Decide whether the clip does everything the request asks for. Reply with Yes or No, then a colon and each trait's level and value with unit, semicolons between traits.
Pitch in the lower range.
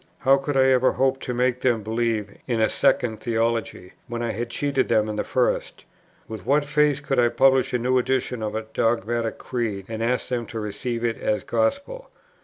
Yes: low, 120 Hz